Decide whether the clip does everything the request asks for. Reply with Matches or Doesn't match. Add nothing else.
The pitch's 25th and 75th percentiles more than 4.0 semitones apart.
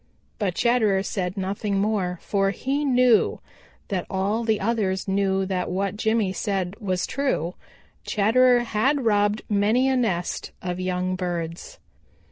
Doesn't match